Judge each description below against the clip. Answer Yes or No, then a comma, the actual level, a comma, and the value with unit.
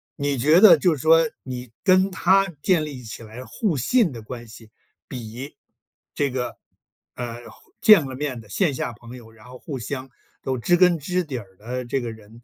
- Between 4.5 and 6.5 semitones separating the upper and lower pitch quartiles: Yes, wide, 5.5 semitones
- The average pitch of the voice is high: No, low, 130 Hz